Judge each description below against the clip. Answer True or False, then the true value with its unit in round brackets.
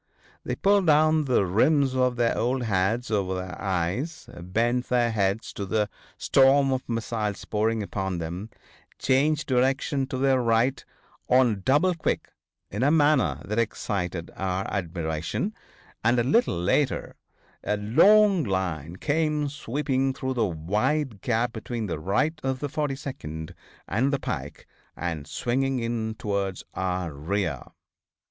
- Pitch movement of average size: False (5.9 semitones)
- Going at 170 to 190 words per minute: False (140 wpm)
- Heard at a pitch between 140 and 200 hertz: False (115 Hz)